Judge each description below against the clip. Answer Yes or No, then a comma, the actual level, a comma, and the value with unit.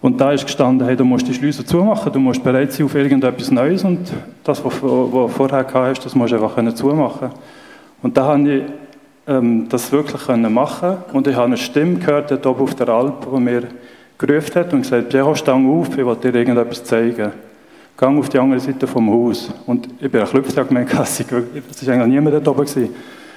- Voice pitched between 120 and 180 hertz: Yes, low, 135 Hz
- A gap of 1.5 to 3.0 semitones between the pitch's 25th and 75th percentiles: Yes, average, 2.7 semitones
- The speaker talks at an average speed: No, fast, 210 wpm